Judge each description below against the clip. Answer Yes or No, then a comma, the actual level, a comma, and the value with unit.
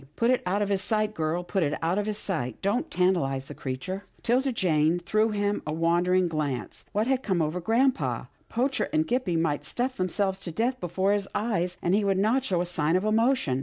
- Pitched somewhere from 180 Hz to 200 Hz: Yes, high, 190 Hz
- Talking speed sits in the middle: No, fast, 220 wpm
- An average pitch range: Yes, average, 4.6 semitones